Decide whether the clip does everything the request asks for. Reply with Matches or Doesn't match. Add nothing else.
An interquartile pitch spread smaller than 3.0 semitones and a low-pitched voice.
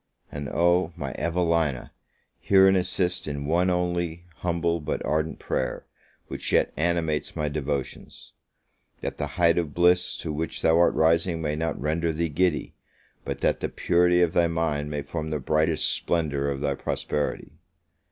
Matches